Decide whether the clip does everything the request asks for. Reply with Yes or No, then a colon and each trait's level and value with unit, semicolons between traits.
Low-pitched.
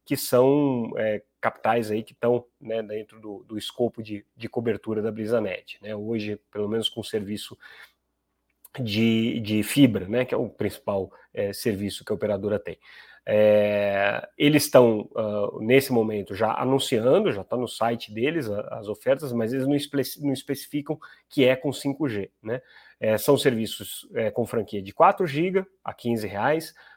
Yes: low, 115 Hz